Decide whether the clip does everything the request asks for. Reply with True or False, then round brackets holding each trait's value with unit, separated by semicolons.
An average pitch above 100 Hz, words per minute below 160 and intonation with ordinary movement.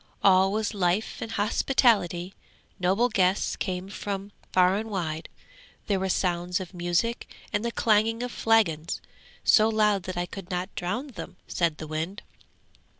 True (190 Hz; 150 wpm; 3.3 semitones)